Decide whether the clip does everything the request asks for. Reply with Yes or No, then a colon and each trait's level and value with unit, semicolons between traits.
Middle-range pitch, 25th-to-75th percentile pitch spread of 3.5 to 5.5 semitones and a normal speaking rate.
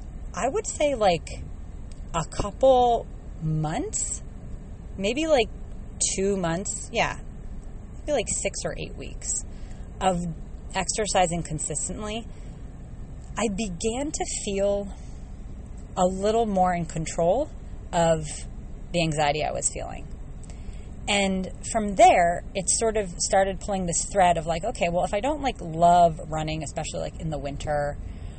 No: medium, 180 Hz; average, 4.8 semitones; slow, 130 wpm